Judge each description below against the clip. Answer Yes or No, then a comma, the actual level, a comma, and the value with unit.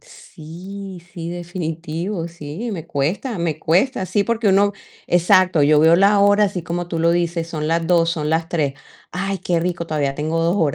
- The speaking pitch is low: No, medium, 170 Hz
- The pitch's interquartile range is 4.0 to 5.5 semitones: No, average, 2.8 semitones